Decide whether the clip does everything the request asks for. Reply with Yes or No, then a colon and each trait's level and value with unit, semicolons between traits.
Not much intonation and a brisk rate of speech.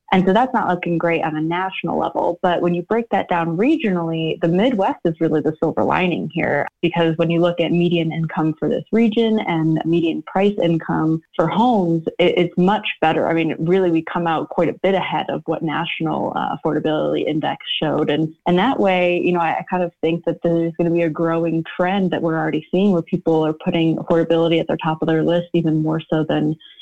Yes: narrow, 1.9 semitones; fast, 215 wpm